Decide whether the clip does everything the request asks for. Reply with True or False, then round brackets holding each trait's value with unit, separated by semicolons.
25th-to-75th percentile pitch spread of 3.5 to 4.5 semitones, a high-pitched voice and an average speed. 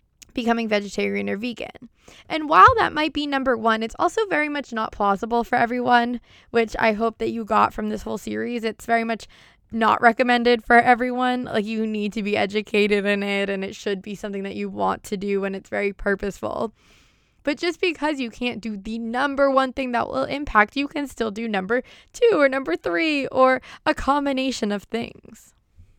True (4.1 semitones; 230 Hz; 195 wpm)